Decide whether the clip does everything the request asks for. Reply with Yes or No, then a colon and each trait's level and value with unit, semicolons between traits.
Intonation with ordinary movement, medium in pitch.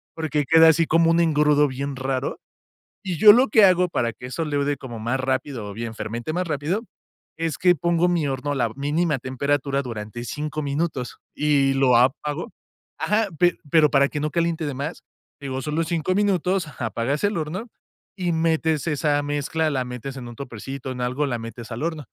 Yes: average, 4.0 semitones; medium, 145 Hz